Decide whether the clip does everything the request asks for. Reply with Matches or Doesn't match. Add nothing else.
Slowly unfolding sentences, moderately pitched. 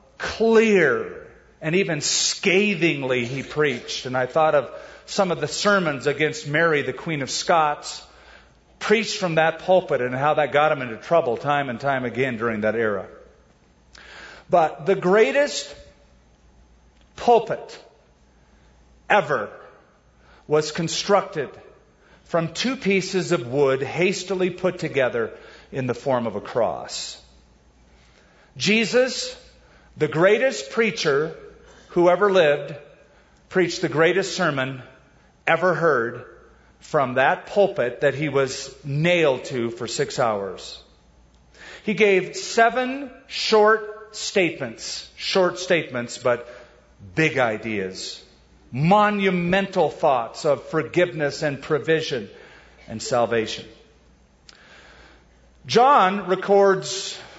Matches